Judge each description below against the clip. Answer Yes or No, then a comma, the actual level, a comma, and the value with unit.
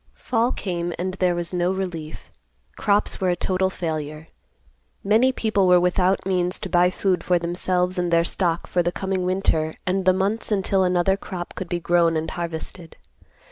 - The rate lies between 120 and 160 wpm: No, average, 180 wpm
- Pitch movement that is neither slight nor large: No, narrow, 1.7 semitones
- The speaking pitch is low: No, medium, 180 Hz